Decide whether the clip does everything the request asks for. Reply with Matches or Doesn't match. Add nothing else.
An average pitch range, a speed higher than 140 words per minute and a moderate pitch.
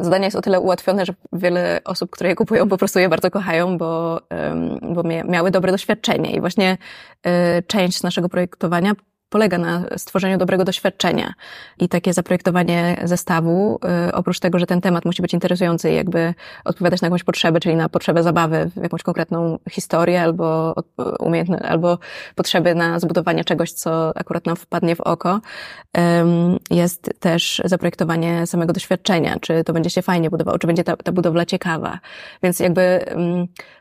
Doesn't match